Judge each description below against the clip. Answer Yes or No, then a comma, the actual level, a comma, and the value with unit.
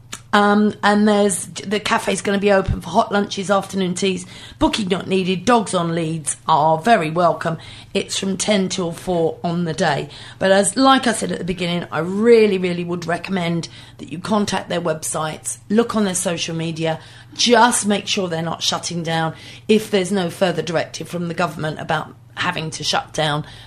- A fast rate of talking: No, average, 190 wpm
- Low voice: No, medium, 175 Hz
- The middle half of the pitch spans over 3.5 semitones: Yes, average, 4.0 semitones